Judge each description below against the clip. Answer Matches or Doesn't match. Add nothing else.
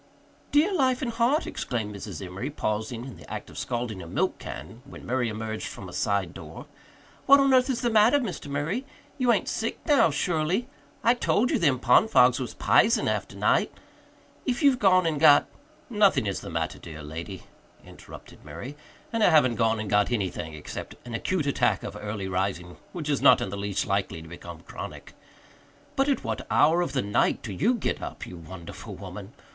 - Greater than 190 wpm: Matches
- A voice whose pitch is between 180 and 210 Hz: Doesn't match